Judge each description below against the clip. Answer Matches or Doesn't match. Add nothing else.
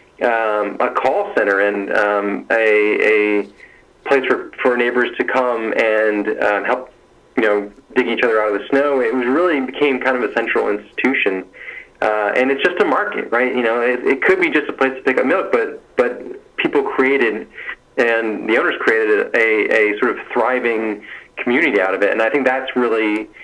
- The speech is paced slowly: Doesn't match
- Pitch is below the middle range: Matches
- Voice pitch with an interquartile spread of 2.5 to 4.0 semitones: Doesn't match